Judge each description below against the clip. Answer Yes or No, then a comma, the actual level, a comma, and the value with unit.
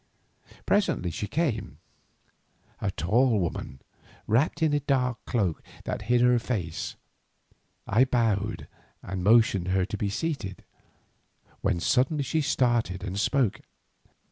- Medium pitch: No, low, 115 Hz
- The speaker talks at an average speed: No, slow, 125 wpm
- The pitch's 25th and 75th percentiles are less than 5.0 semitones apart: No, average, 5.3 semitones